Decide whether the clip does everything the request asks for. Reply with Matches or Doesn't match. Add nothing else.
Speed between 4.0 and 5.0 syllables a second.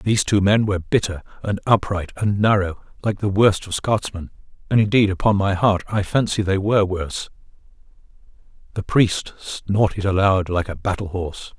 Doesn't match